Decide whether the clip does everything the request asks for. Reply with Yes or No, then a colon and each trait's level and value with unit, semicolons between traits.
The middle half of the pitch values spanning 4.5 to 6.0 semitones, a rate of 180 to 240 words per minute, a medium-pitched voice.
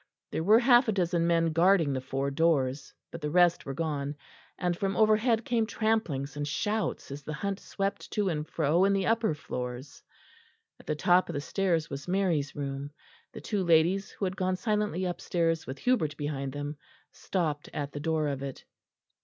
Yes: average, 5.2 semitones; average, 185 wpm; medium, 165 Hz